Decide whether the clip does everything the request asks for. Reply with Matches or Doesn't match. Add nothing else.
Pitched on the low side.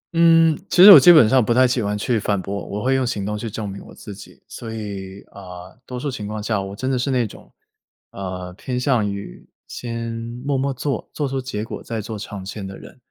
Matches